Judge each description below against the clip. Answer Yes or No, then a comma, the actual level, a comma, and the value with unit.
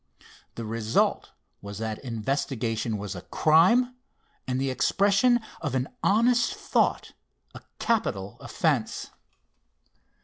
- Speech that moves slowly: Yes, slow, 105 wpm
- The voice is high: No, low, 130 Hz